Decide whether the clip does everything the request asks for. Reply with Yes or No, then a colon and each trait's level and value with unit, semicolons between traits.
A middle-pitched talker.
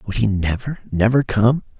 No: low, 110 Hz